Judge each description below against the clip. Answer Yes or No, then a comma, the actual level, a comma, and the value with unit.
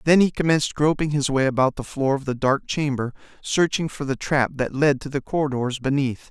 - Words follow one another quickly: Yes, fast, 220 wpm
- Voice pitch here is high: No, medium, 140 Hz